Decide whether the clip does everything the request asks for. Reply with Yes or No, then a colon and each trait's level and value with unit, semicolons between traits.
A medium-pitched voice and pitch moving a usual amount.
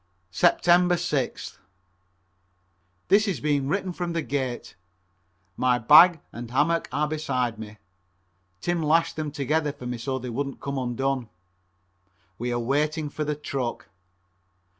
Yes: medium, 145 Hz; average, 4.1 semitones